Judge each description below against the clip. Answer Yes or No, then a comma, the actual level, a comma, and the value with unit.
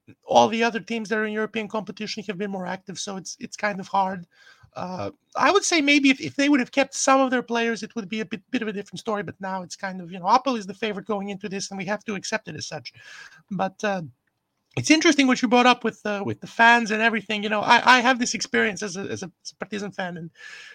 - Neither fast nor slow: No, fast, 280 wpm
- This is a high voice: Yes, high, 215 Hz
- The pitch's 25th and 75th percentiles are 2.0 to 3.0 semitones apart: No, average, 3.4 semitones